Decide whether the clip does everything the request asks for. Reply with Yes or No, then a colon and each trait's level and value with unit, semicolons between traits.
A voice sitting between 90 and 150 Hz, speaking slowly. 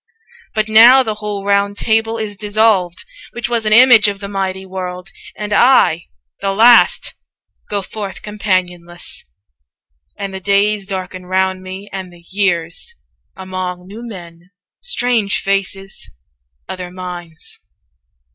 No: high, 195 Hz; slow, 130 wpm